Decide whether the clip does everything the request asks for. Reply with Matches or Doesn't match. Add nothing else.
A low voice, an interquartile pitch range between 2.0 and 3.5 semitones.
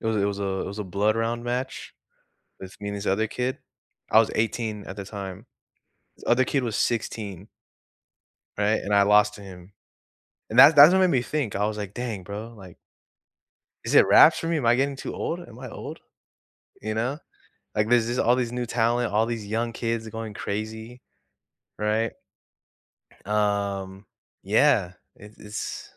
Matches